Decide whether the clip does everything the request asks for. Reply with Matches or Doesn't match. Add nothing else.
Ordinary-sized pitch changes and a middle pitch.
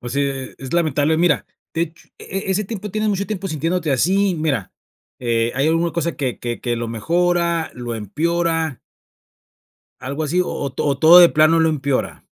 Matches